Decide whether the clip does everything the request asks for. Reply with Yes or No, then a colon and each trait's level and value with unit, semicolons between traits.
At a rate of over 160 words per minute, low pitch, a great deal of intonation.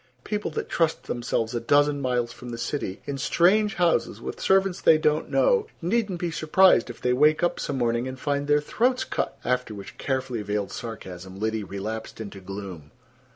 Yes: average, 185 wpm; low, 130 Hz; wide, 6.7 semitones